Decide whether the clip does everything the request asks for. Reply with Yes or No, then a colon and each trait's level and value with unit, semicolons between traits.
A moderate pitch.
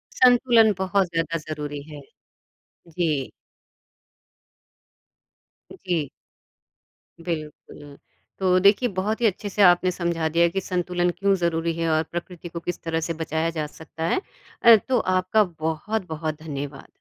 Yes: medium, 170 Hz